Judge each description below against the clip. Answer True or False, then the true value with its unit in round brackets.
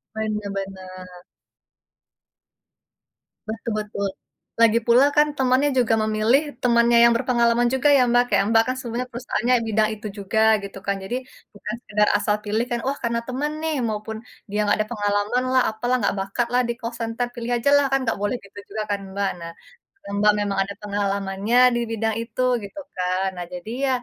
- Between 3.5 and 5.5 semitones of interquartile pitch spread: False (3.1 semitones)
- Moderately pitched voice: False (220 Hz)